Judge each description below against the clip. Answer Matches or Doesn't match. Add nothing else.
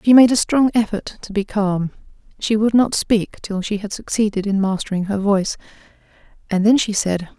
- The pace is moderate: Matches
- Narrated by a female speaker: Matches